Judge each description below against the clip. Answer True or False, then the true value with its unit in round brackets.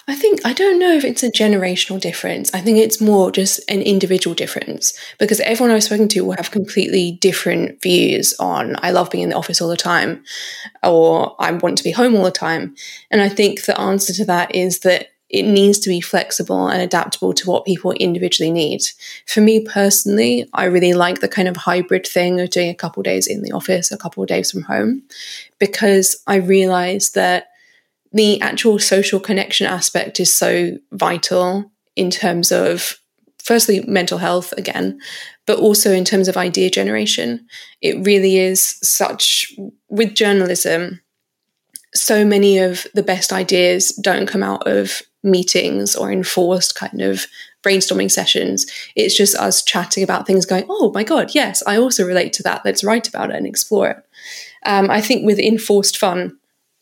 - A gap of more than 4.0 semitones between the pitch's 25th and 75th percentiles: False (2.9 semitones)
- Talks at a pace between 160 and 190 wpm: True (180 wpm)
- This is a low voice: False (195 Hz)